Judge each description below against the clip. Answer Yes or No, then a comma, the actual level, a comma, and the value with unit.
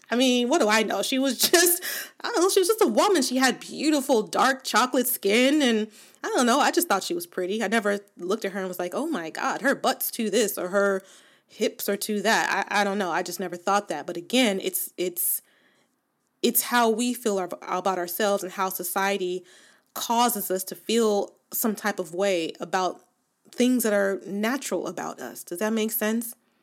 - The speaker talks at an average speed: No, fast, 215 wpm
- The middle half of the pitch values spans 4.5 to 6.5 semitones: Yes, average, 5.1 semitones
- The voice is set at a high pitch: Yes, high, 210 Hz